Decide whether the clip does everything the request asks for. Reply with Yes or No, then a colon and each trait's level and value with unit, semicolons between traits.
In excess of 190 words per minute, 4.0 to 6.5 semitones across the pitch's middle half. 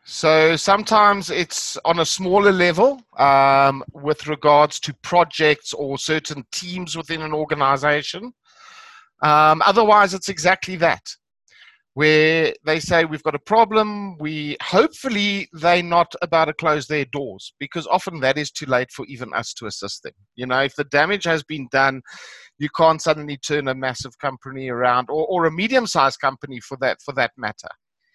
No: average, 165 wpm; average, 4.5 semitones